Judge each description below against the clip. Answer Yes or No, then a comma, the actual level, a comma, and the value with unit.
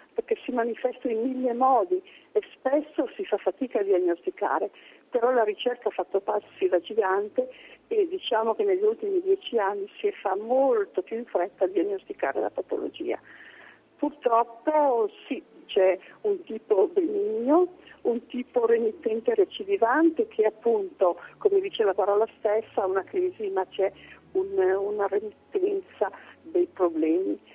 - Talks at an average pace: Yes, average, 145 wpm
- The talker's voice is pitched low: No, very high, 295 Hz